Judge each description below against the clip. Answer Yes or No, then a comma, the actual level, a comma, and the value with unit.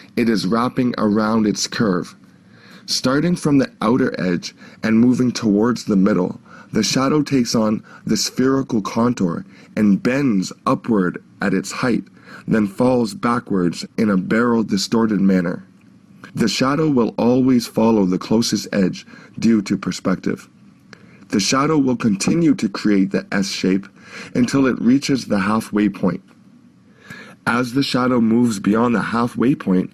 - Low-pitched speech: Yes, low, 115 Hz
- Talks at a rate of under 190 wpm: Yes, average, 140 wpm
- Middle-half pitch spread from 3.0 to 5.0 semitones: Yes, average, 3.5 semitones